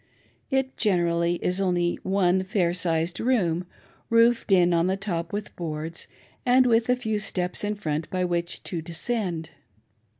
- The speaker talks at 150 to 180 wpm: Yes, average, 155 wpm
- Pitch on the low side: No, medium, 180 Hz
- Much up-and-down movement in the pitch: No, average, 3.8 semitones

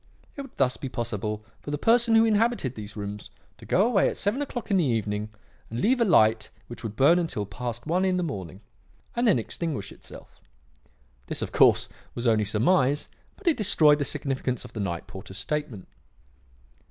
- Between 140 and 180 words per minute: No, average, 190 wpm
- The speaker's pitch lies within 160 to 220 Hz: No, low, 130 Hz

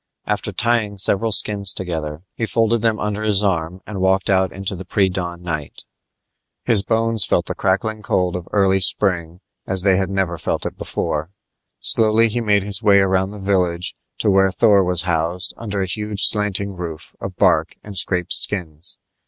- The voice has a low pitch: Yes, very low, 95 Hz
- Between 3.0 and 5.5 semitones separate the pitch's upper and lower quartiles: No, narrow, 2.6 semitones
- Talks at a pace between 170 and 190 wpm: Yes, average, 180 wpm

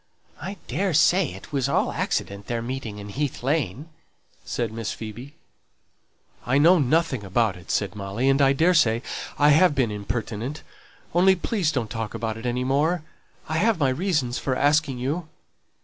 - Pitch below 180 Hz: Yes, low, 135 Hz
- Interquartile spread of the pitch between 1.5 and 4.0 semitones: No, wide, 5.6 semitones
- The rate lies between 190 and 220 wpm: No, average, 165 wpm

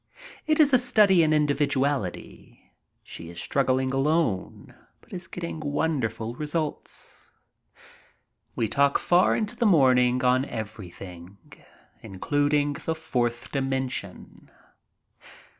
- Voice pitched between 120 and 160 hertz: Yes, medium, 140 Hz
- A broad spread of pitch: No, average, 4.9 semitones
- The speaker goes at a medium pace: No, slow, 110 wpm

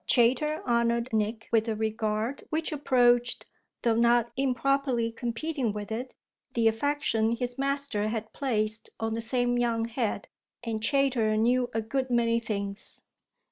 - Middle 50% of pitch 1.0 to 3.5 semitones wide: Yes, narrow, 2.4 semitones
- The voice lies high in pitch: Yes, high, 235 Hz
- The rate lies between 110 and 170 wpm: Yes, average, 140 wpm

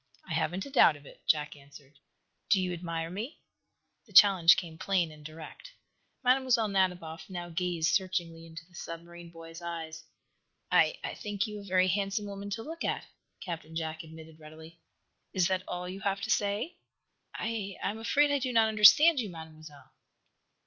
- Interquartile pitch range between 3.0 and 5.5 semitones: Yes, average, 4.1 semitones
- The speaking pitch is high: No, medium, 180 Hz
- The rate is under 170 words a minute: No, average, 175 wpm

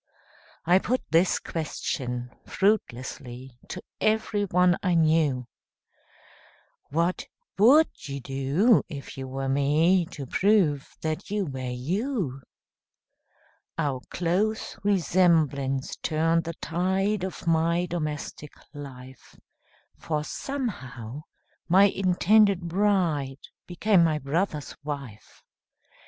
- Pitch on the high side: No, medium, 165 Hz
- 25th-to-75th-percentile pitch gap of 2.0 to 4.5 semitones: No, wide, 5.5 semitones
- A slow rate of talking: Yes, slow, 95 wpm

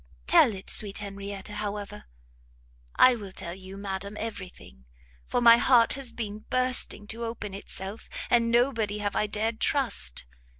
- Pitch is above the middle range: Yes, high, 210 Hz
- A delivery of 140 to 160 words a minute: Yes, average, 155 wpm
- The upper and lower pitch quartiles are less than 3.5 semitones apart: Yes, average, 2.8 semitones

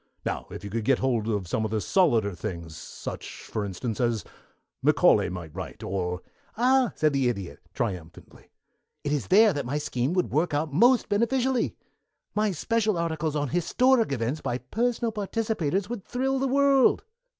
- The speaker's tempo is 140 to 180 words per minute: Yes, average, 170 wpm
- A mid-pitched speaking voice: Yes, medium, 150 Hz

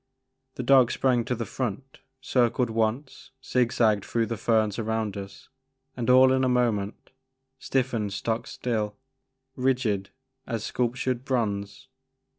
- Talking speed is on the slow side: Yes, slow, 130 wpm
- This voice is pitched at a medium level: No, low, 120 Hz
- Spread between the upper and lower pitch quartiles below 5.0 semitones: Yes, average, 2.9 semitones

